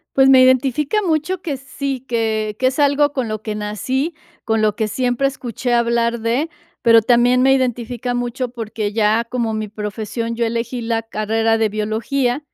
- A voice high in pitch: Yes, high, 235 Hz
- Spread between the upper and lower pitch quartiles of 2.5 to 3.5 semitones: Yes, average, 2.8 semitones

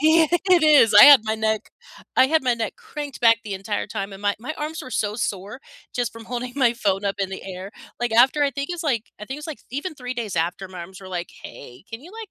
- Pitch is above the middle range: Yes, high, 235 Hz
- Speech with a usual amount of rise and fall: No, wide, 6.1 semitones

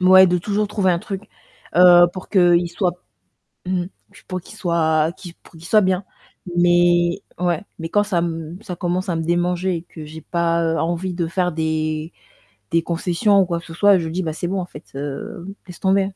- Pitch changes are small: Yes, narrow, 1.9 semitones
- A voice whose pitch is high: No, medium, 175 Hz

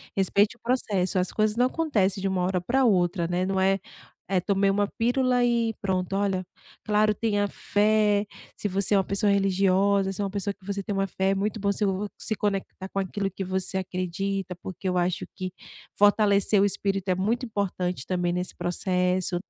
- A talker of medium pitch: No, high, 195 Hz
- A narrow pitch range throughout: Yes, narrow, 1.8 semitones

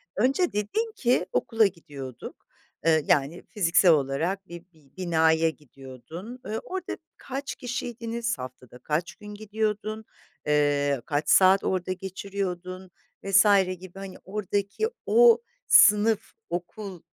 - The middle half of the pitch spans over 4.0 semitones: Yes, average, 5.2 semitones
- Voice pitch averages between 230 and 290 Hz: No, high, 190 Hz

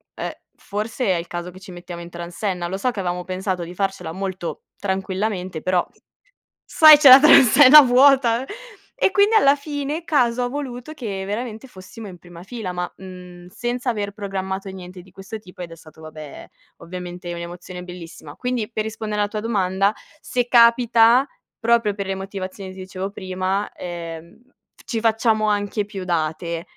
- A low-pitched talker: No, high, 195 Hz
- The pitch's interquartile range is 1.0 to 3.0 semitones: No, average, 4.6 semitones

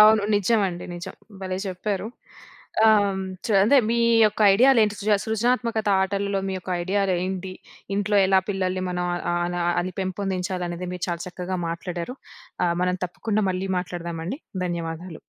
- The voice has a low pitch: No, high, 190 Hz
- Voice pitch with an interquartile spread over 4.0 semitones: No, average, 2.7 semitones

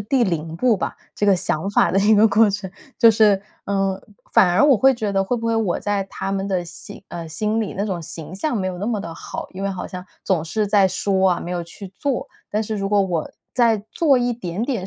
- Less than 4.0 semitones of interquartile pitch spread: Yes, average, 2.9 semitones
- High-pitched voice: Yes, high, 200 Hz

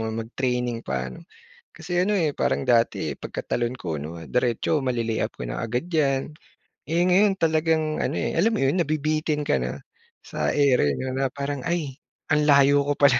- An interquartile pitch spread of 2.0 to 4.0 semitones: No, average, 5.1 semitones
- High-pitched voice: No, medium, 140 Hz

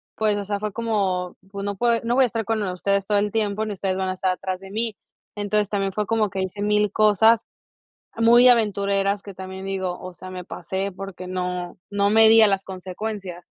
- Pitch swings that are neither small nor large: No, narrow, 2.2 semitones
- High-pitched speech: Yes, high, 200 Hz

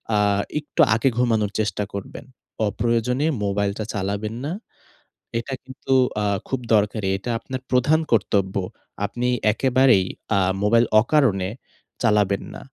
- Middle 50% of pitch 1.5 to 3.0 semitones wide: No, average, 3.7 semitones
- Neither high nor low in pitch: No, low, 110 Hz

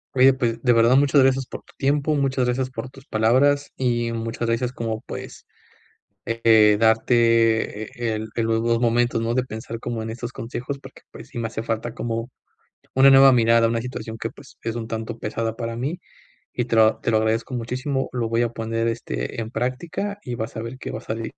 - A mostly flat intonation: Yes, narrow, 2.1 semitones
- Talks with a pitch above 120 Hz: No, low, 115 Hz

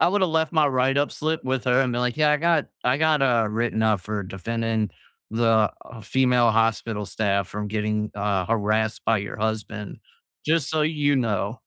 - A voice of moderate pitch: No, low, 115 Hz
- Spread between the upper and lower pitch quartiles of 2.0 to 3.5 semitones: No, average, 4.6 semitones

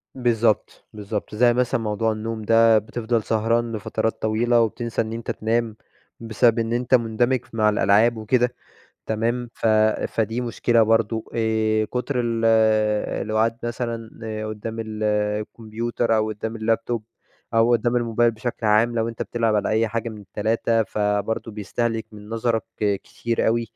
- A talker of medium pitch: No, low, 115 Hz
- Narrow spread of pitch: Yes, narrow, 1.4 semitones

